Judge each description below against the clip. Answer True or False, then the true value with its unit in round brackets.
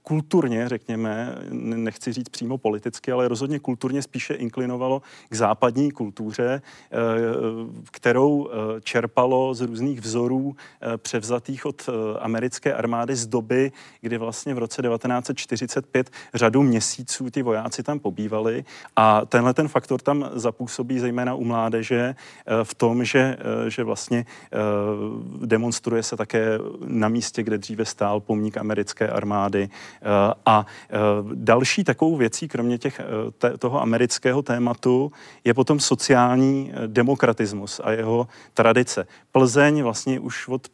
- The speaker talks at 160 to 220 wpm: False (120 wpm)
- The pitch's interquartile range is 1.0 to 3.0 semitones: True (2.5 semitones)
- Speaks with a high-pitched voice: False (120 Hz)